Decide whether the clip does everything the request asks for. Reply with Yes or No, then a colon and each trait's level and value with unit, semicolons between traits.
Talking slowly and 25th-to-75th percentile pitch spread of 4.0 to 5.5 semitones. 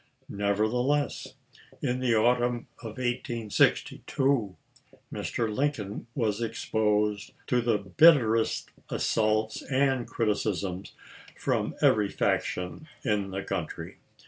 No: slow, 90 wpm; average, 3.1 semitones